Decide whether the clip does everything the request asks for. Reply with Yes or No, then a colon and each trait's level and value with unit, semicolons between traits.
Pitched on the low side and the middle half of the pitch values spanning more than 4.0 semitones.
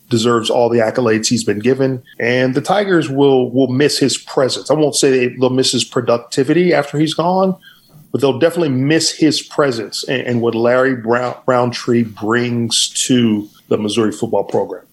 No: low, 130 Hz; average, 3.2 semitones